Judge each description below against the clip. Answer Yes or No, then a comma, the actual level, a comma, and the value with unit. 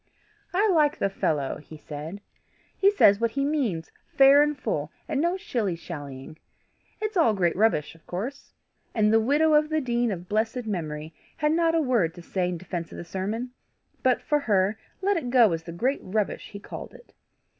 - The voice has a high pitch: Yes, high, 220 Hz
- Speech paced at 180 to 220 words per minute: Yes, average, 195 wpm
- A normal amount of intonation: No, wide, 8.6 semitones